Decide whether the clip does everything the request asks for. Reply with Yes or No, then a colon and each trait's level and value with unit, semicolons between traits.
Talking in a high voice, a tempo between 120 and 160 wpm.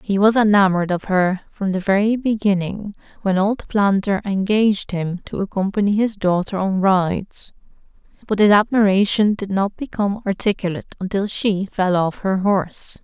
Yes: high, 200 Hz; average, 150 wpm